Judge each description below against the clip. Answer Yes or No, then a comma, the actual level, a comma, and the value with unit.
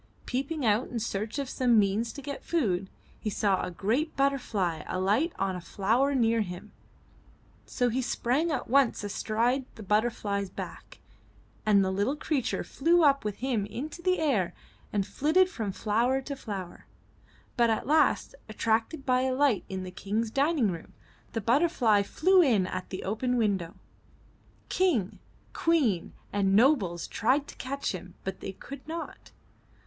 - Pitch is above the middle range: Yes, high, 230 Hz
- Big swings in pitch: Yes, wide, 5.7 semitones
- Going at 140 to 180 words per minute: Yes, average, 160 wpm